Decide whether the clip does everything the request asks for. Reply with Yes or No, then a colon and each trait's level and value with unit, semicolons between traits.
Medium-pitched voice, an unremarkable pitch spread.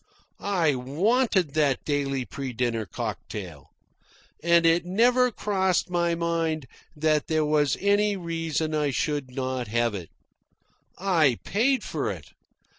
Yes: medium, 155 Hz; average, 5.0 semitones